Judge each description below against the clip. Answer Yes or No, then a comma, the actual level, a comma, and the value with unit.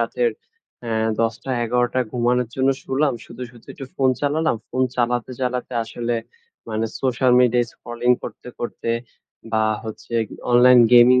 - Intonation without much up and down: Yes, narrow, 1.4 semitones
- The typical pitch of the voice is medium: No, low, 125 Hz